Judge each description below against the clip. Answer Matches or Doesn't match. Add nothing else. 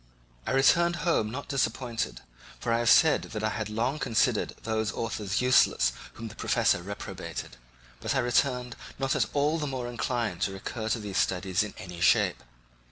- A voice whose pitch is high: Doesn't match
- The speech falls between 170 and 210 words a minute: Matches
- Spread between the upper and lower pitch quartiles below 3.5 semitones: Doesn't match